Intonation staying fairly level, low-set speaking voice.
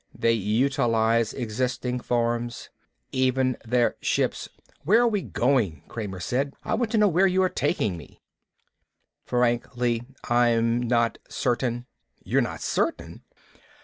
Yes: narrow, 2.2 semitones; low, 120 Hz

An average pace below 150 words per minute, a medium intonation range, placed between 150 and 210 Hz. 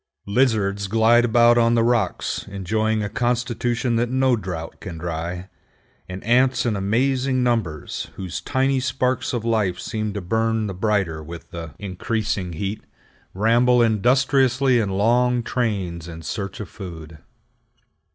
No: average, 140 wpm; average, 4.2 semitones; low, 110 Hz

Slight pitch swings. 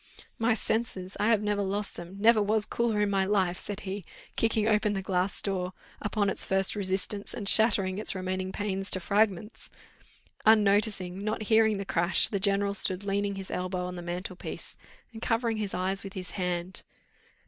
Yes: narrow, 2.1 semitones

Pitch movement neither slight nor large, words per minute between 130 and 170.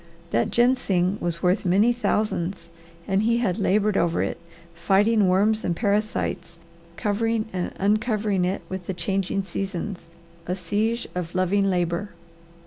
Yes: average, 3.0 semitones; slow, 135 wpm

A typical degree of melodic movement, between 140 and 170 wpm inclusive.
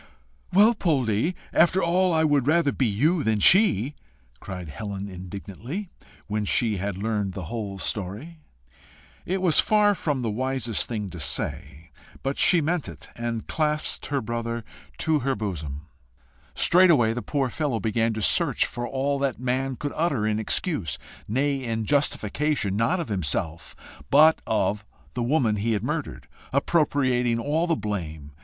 No: wide, 6.4 semitones; average, 155 wpm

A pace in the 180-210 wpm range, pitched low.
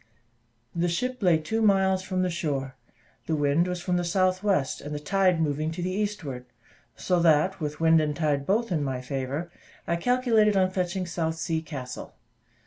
No: average, 185 wpm; medium, 170 Hz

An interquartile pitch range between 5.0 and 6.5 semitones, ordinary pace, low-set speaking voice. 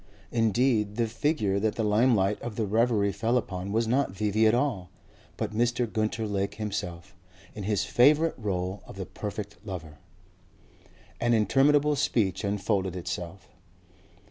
No: average, 3.3 semitones; average, 145 wpm; low, 105 Hz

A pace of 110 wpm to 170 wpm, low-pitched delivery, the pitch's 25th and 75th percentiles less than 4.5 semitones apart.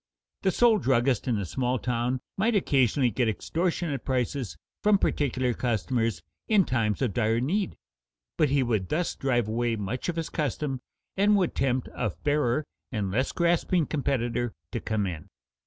No: average, 160 wpm; low, 130 Hz; average, 4.9 semitones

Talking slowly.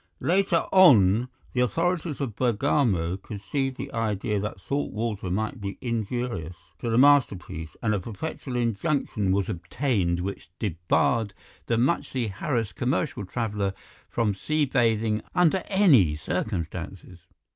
Yes: slow, 125 wpm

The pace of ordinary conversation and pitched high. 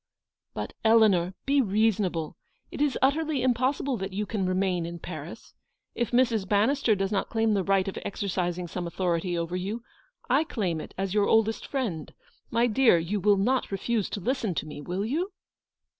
Yes: average, 175 wpm; high, 205 Hz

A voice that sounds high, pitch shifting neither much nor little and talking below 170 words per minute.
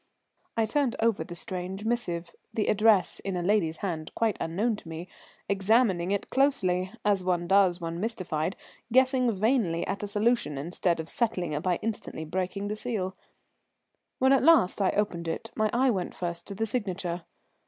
No: high, 195 Hz; average, 4.4 semitones; average, 175 wpm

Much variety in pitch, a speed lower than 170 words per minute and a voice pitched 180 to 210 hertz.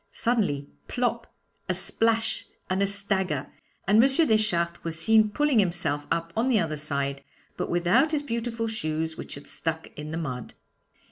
Yes: wide, 6.2 semitones; average, 160 wpm; high, 190 Hz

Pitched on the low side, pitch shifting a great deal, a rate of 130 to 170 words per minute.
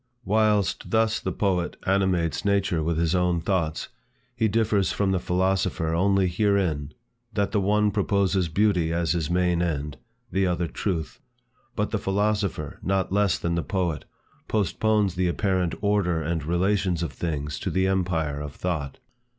No: very low, 90 Hz; average, 3.1 semitones; average, 155 wpm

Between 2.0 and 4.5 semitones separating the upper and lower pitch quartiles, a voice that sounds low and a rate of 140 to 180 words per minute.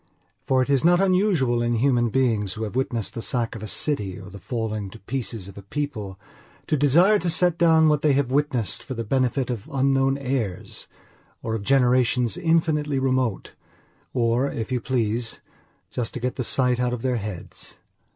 No: average, 3.7 semitones; low, 125 Hz; average, 190 wpm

